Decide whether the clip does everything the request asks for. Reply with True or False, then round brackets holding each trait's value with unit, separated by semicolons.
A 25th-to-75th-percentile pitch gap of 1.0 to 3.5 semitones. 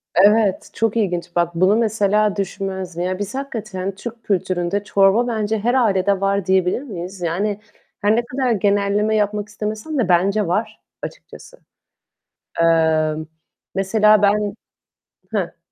True (2.4 semitones)